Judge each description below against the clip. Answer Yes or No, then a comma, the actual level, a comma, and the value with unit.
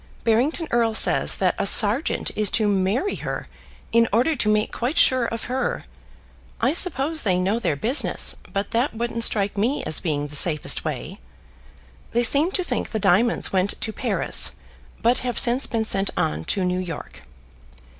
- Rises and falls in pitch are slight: No, average, 4.2 semitones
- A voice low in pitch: No, high, 225 Hz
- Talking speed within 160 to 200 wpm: Yes, average, 175 wpm